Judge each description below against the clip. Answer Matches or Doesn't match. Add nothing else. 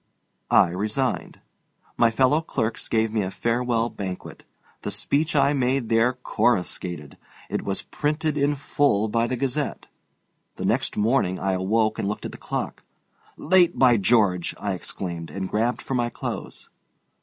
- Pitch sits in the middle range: Doesn't match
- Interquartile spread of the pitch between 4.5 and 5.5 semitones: Matches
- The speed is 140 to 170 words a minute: Matches